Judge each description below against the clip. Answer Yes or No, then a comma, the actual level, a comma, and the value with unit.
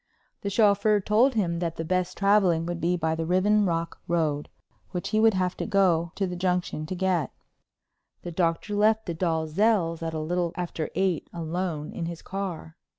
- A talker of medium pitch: Yes, medium, 180 Hz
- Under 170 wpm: No, average, 185 wpm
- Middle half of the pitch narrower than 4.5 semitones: Yes, average, 3.0 semitones